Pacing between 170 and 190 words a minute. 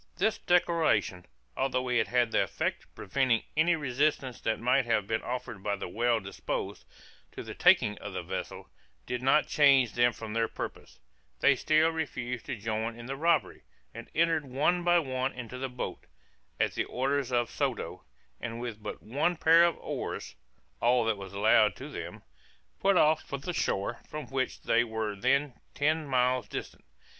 Yes: average, 175 wpm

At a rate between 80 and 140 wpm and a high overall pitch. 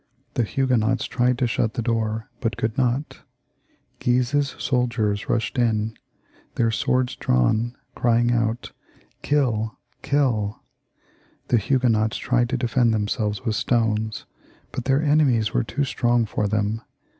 No: slow, 135 wpm; low, 120 Hz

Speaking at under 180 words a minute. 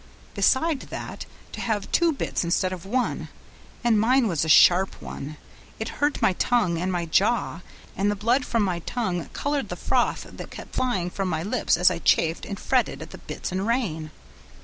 No: average, 195 wpm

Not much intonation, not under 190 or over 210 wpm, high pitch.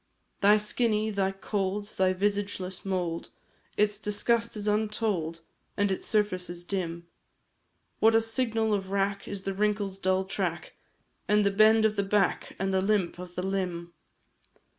No: narrow, 2.0 semitones; average, 155 wpm; high, 200 Hz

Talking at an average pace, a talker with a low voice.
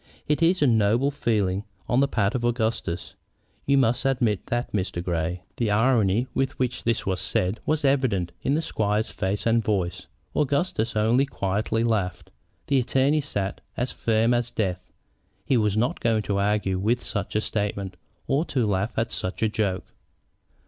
Yes: average, 170 wpm; low, 110 Hz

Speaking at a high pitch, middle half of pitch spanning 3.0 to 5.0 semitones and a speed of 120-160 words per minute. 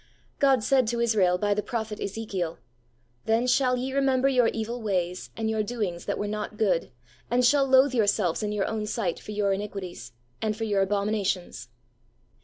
No: high, 215 Hz; average, 3.6 semitones; average, 185 wpm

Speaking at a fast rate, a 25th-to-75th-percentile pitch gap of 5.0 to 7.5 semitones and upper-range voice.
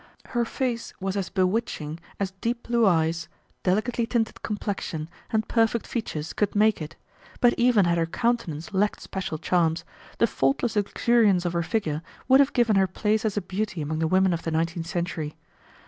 No: average, 180 wpm; wide, 5.4 semitones; high, 195 Hz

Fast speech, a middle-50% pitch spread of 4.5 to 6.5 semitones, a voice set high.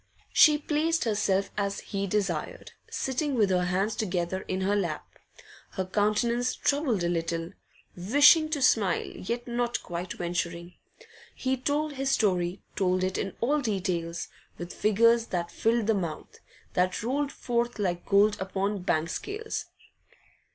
No: average, 150 wpm; average, 5.1 semitones; high, 205 Hz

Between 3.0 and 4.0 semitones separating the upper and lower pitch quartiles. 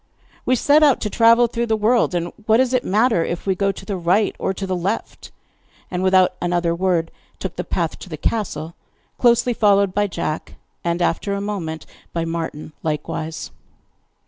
No: average, 4.7 semitones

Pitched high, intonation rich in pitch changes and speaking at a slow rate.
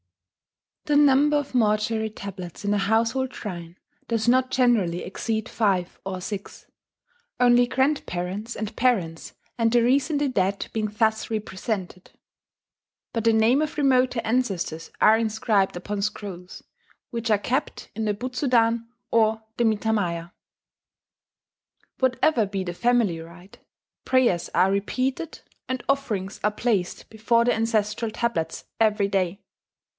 No: high, 220 Hz; average, 3.7 semitones; slow, 130 wpm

